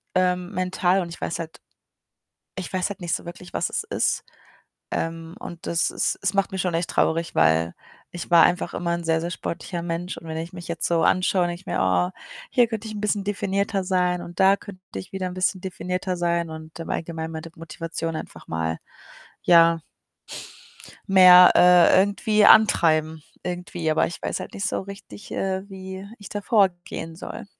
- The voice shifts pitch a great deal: No, narrow, 2.4 semitones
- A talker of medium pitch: Yes, medium, 180 Hz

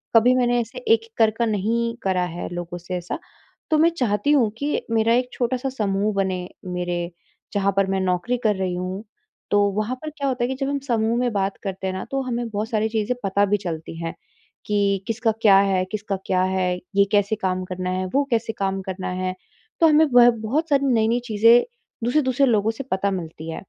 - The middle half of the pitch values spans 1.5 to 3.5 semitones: No, average, 4.3 semitones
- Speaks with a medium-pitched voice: No, high, 210 Hz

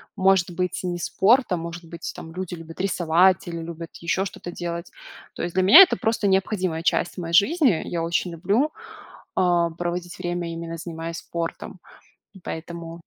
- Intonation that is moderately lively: No, narrow, 1.9 semitones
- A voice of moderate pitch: Yes, medium, 175 Hz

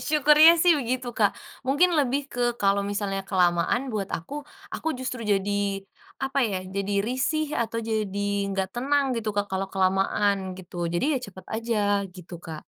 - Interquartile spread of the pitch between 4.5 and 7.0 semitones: Yes, average, 5.1 semitones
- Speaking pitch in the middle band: No, high, 215 Hz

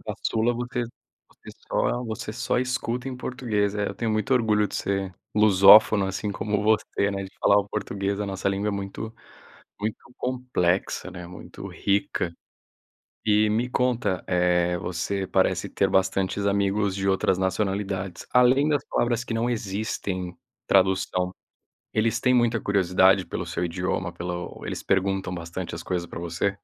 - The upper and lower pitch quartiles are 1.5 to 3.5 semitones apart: Yes, average, 2.9 semitones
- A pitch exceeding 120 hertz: No, low, 100 Hz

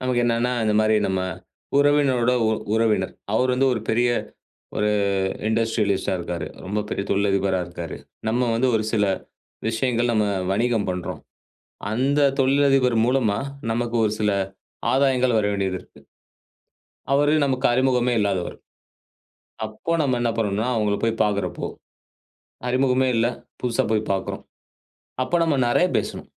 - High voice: No, low, 115 Hz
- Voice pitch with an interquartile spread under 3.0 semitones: No, average, 3.6 semitones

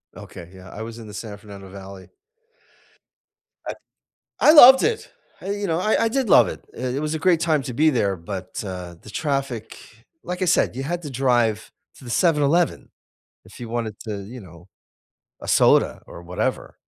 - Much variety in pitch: Yes, wide, 8.6 semitones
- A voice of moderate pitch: No, low, 125 Hz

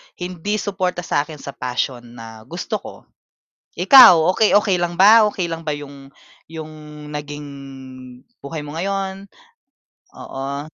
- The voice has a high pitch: No, medium, 165 Hz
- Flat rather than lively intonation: No, average, 5.0 semitones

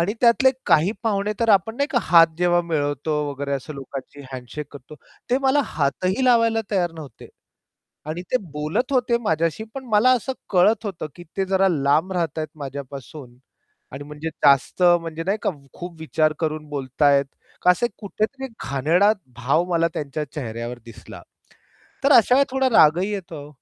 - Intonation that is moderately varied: No, wide, 6.5 semitones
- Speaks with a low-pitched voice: No, medium, 165 Hz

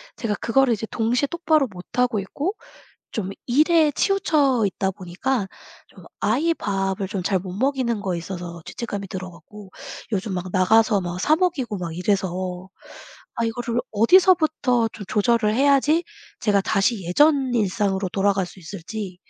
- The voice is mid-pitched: No, high, 210 Hz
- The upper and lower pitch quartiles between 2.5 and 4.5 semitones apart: No, wide, 5.5 semitones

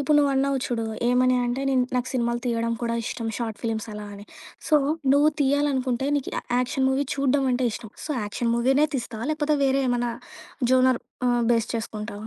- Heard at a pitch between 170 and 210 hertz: No, very high, 250 Hz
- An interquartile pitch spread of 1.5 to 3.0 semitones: Yes, average, 2.7 semitones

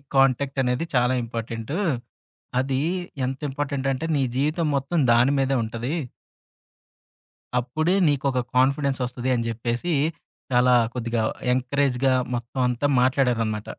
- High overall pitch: No, low, 130 Hz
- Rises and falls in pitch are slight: Yes, narrow, 2.2 semitones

